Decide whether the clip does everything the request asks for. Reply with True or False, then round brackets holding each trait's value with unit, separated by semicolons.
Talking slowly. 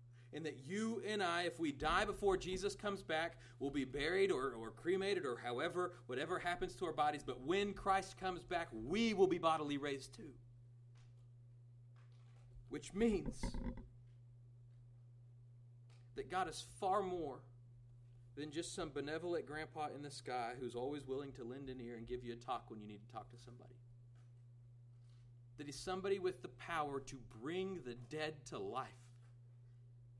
False (165 wpm)